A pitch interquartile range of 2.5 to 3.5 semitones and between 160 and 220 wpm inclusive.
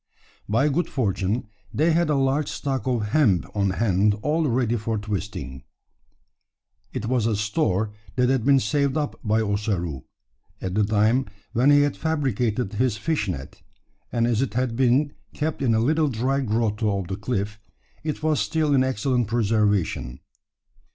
No: average, 4.7 semitones; average, 165 wpm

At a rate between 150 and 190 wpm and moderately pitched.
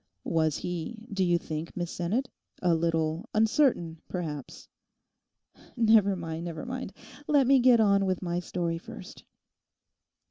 No: slow, 135 wpm; medium, 175 Hz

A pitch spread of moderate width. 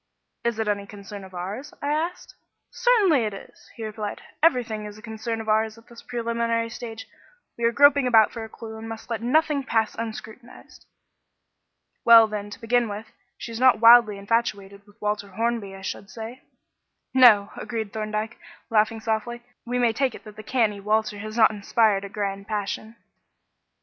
No: narrow, 2.1 semitones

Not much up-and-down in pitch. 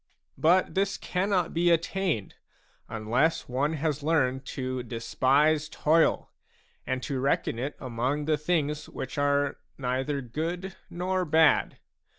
No: average, 4.1 semitones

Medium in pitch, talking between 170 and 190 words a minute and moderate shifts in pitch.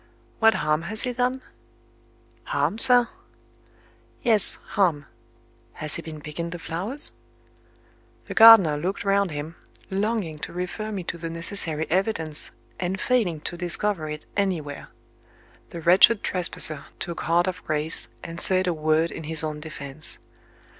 No: medium, 170 Hz; average, 140 wpm; average, 4.4 semitones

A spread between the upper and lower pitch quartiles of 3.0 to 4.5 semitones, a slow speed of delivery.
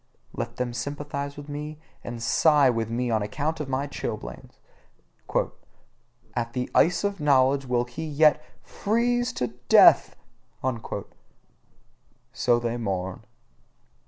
Yes: average, 4.0 semitones; slow, 120 wpm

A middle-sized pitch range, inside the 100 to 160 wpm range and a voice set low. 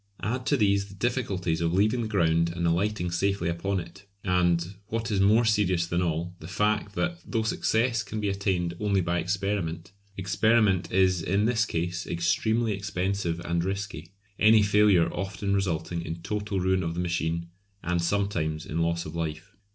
No: average, 3.4 semitones; average, 175 wpm; very low, 95 Hz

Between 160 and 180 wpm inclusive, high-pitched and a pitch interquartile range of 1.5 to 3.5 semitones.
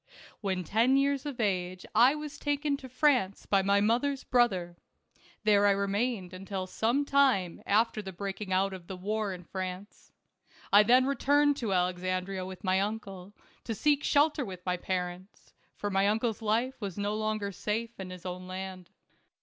No: average, 170 wpm; high, 205 Hz; average, 4.5 semitones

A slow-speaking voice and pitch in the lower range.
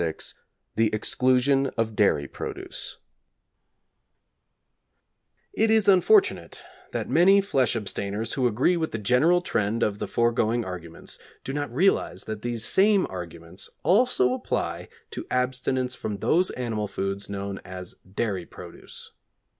Yes: slow, 130 wpm; low, 120 Hz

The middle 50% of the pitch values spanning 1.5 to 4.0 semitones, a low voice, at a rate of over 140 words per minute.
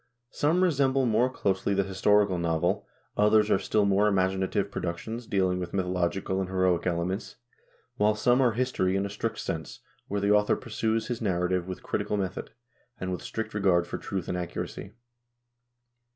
Yes: average, 2.9 semitones; low, 100 Hz; average, 165 wpm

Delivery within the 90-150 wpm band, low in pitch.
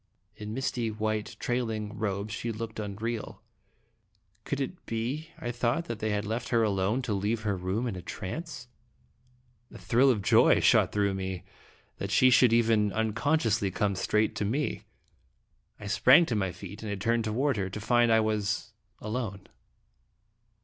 No: average, 165 wpm; low, 110 Hz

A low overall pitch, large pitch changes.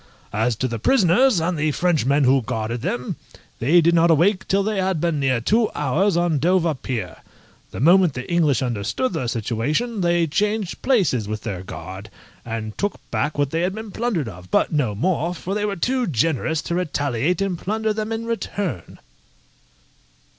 No: medium, 165 Hz; wide, 7.3 semitones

